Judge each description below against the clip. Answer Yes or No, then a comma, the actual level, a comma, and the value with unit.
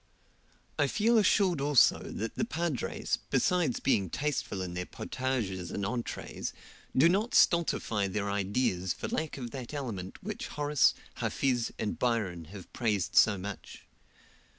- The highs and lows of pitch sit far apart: Yes, wide, 7.1 semitones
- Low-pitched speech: Yes, low, 120 Hz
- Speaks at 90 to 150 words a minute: Yes, average, 140 wpm